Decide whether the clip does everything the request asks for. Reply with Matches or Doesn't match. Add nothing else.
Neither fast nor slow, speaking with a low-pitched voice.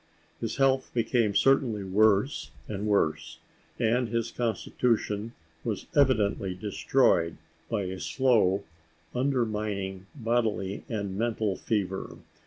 Doesn't match